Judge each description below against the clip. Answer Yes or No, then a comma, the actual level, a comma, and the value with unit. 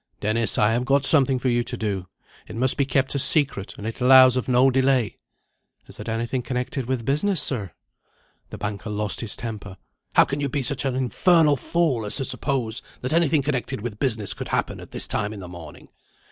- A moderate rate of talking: No, fast, 210 wpm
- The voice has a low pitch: Yes, low, 125 Hz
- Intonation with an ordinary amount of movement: Yes, average, 3.9 semitones